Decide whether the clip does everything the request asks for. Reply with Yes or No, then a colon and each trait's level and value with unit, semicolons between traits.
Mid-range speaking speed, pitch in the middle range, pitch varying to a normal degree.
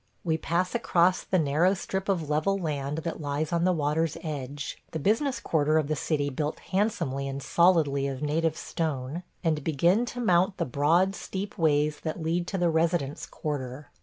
Yes: average, 190 wpm; medium, 160 Hz; average, 3.7 semitones